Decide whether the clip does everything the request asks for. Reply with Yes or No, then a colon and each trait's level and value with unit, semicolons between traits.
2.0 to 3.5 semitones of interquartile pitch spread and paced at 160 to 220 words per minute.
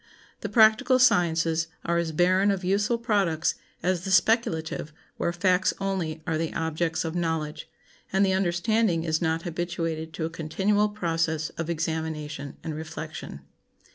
No: average, 3.2 semitones; average, 145 wpm